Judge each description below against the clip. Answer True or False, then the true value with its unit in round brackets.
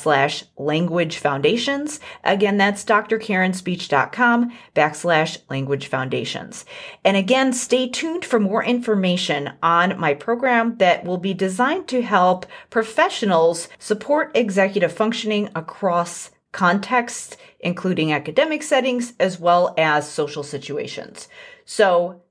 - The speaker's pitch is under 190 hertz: False (195 Hz)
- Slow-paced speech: True (105 wpm)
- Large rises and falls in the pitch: True (6.0 semitones)